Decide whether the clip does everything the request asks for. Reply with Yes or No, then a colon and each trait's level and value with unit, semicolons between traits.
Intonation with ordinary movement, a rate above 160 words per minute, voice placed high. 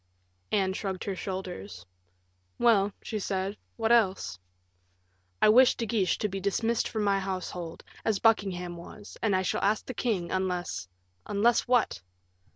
No: average, 3.1 semitones; average, 155 wpm; high, 195 Hz